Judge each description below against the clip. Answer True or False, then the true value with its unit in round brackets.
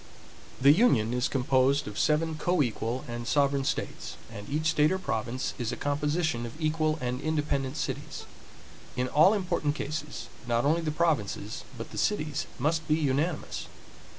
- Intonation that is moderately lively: True (3.7 semitones)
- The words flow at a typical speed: True (155 wpm)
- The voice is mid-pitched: True (145 Hz)